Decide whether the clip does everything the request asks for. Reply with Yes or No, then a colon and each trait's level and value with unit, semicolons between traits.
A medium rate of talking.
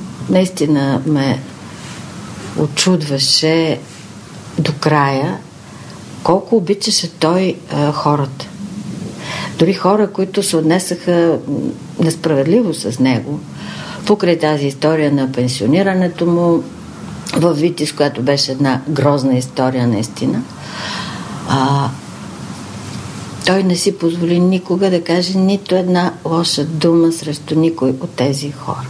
No: slow, 100 wpm